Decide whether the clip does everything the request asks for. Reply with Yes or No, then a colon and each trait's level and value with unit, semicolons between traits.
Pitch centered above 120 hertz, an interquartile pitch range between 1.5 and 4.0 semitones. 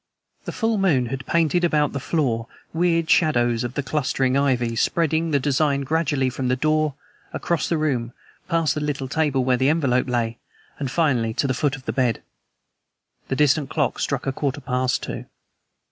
Yes: medium, 140 Hz; average, 3.5 semitones